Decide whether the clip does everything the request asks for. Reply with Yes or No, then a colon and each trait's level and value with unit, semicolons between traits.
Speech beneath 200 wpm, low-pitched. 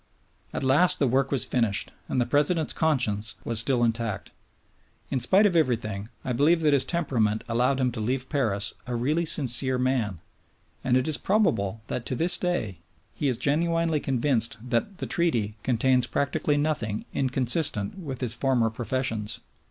Yes: average, 165 wpm; low, 130 Hz